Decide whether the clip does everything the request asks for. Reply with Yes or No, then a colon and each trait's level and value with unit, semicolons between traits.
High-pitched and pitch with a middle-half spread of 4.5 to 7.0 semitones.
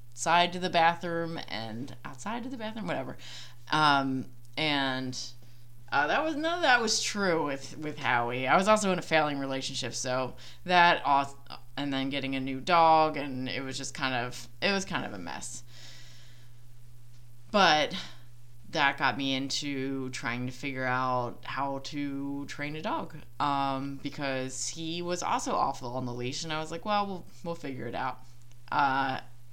No: low, 135 Hz; average, 4.9 semitones